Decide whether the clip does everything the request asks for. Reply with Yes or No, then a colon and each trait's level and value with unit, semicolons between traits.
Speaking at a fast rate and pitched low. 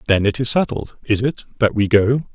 Yes: fast, 230 wpm; low, 115 Hz